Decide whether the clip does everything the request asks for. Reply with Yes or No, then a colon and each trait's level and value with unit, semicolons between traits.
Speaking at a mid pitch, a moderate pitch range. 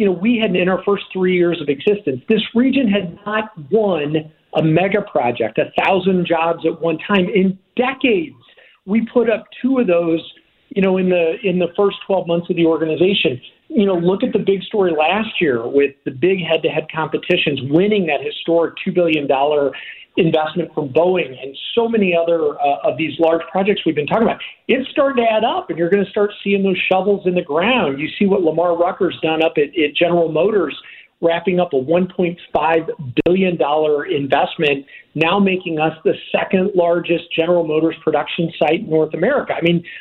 Yes: medium, 175 Hz; average, 4.0 semitones